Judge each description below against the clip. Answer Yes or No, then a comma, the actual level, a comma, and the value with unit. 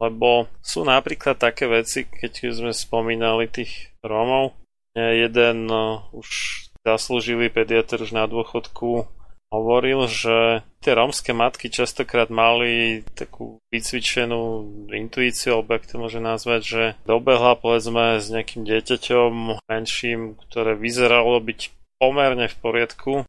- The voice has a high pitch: No, low, 115 Hz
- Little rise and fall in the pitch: Yes, narrow, 1.1 semitones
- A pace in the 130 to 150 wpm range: No, average, 115 wpm